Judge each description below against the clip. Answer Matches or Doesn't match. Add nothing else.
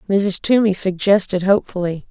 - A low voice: Doesn't match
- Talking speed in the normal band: Doesn't match